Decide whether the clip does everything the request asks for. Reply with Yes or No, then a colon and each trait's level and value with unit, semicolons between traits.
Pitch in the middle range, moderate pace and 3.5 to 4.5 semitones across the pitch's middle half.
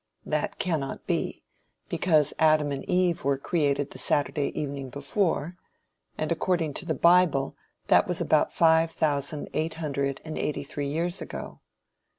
No: medium, 155 Hz; average, 150 wpm; average, 2.9 semitones